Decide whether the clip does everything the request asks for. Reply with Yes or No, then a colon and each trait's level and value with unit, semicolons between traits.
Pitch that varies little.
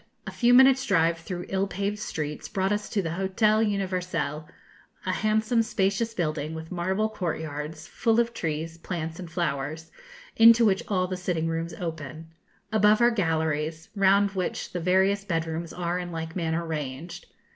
No: average, 3.7 semitones